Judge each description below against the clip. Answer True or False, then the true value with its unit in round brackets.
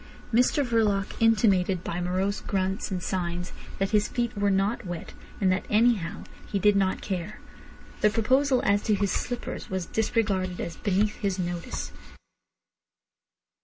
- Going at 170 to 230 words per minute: False (140 wpm)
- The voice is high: True (200 Hz)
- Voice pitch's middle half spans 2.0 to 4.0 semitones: True (2.7 semitones)